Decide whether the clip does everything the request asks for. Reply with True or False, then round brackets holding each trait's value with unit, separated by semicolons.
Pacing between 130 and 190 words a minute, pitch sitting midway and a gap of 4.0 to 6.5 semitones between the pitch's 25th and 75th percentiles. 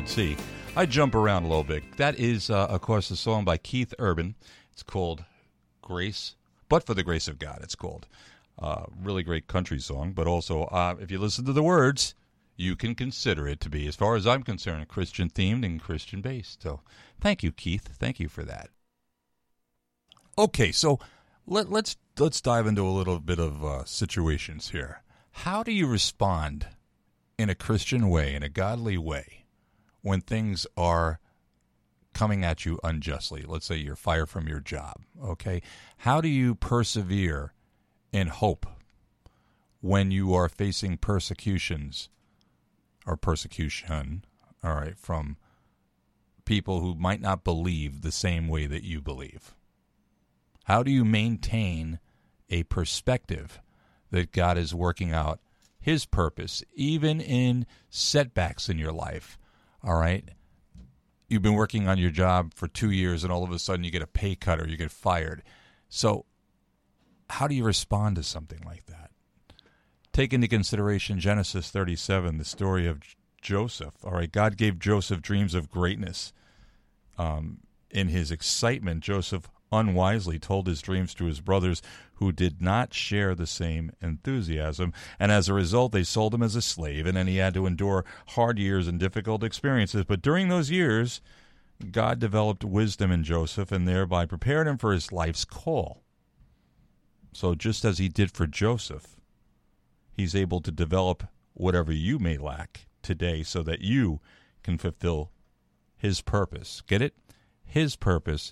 False (160 wpm; 95 Hz; 4.5 semitones)